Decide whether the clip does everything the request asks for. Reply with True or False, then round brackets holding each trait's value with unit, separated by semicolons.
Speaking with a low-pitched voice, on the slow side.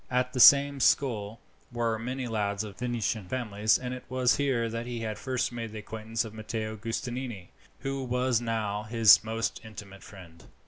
False (115 Hz; 180 wpm)